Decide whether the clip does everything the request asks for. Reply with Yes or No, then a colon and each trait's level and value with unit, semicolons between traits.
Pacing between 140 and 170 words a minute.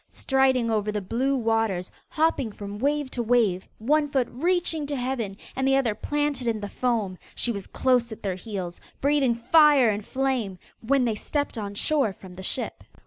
No: average, 185 wpm